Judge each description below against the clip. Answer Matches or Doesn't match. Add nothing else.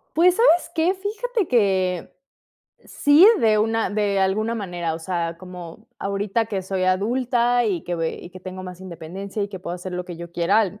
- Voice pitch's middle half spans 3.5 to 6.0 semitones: Matches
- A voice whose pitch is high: Matches